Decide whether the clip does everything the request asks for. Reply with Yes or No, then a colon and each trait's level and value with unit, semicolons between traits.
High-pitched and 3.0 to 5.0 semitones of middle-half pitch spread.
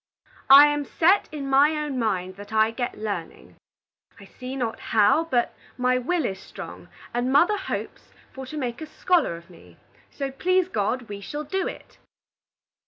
No: very high, 260 Hz; wide, 5.6 semitones